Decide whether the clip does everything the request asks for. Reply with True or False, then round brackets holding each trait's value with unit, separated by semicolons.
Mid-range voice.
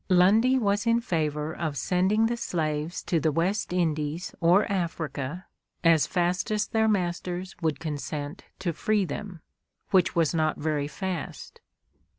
True (175 Hz)